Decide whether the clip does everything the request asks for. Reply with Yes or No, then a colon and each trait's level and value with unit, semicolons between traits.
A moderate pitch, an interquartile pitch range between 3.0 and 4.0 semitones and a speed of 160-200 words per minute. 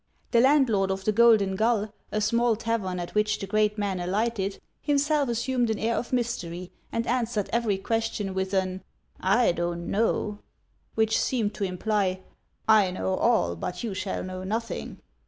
No: high, 210 Hz; average, 3.5 semitones; average, 175 wpm